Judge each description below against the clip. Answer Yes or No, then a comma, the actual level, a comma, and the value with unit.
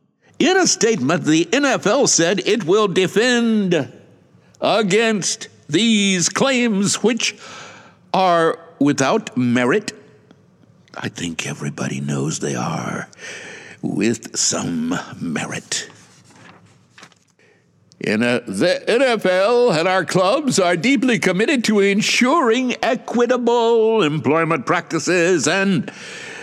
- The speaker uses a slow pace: Yes, slow, 95 wpm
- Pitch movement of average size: No, wide, 6.1 semitones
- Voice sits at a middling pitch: No, high, 210 Hz